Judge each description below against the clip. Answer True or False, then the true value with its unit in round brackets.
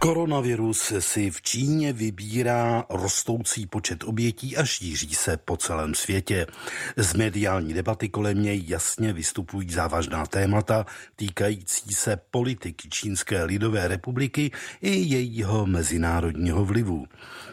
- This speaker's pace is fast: False (115 wpm)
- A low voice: True (105 Hz)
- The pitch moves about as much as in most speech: True (4.7 semitones)